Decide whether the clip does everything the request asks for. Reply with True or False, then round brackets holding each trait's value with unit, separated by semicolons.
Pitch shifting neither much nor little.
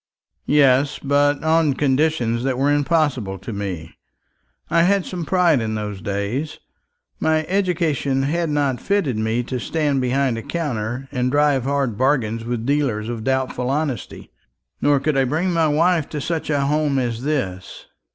True (4.1 semitones)